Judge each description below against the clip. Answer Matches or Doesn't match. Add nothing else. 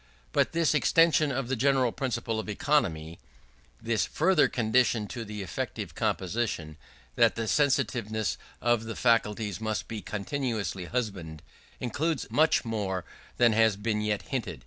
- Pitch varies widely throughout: Doesn't match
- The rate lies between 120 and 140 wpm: Matches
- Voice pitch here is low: Matches